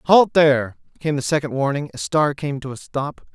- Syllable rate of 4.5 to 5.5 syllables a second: Yes, 5.4 syllables/s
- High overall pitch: No, medium, 145 Hz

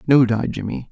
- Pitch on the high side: No, low, 120 Hz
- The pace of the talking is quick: No, average, 195 wpm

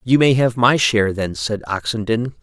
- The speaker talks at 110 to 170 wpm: No, average, 200 wpm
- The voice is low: Yes, low, 115 Hz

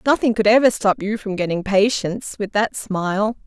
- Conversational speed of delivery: Yes, average, 175 wpm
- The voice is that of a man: No, female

